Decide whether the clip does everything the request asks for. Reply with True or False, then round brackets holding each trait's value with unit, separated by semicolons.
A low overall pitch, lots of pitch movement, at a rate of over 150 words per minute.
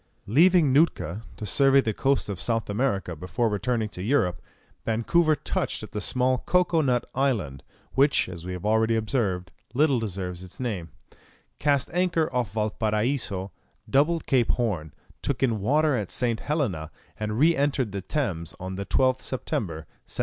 True (115 Hz; 6.1 semitones; 160 wpm)